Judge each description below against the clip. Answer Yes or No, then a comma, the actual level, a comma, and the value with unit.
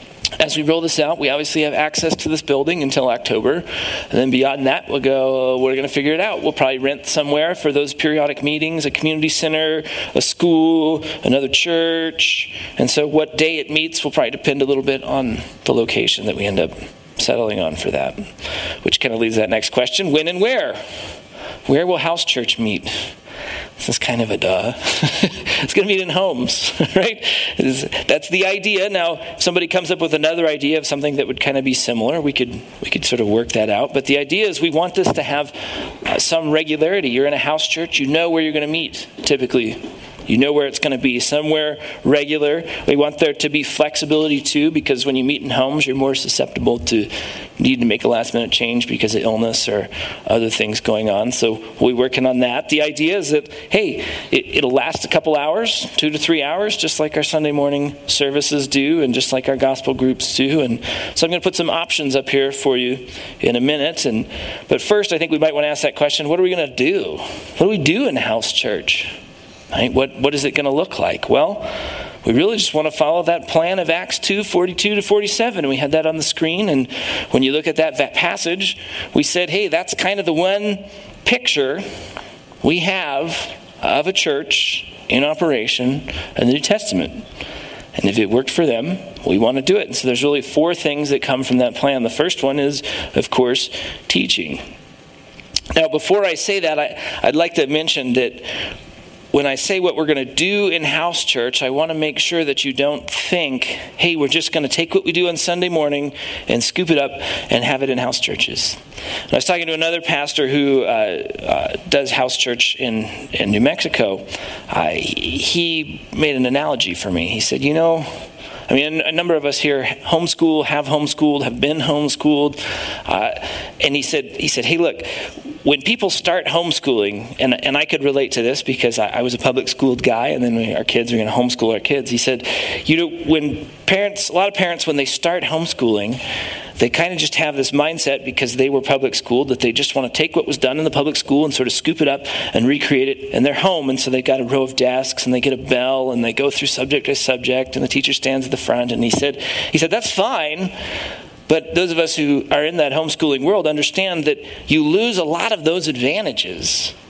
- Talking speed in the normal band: No, fast, 220 wpm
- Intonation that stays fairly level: No, average, 3.6 semitones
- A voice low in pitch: No, medium, 150 Hz